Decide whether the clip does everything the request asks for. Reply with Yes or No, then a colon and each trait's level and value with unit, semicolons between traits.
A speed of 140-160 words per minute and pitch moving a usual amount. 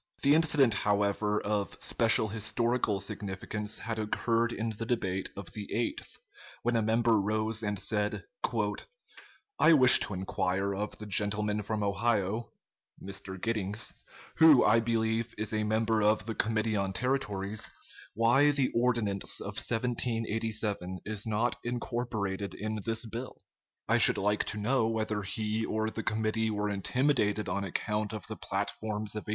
No: average, 150 wpm; narrow, 1.9 semitones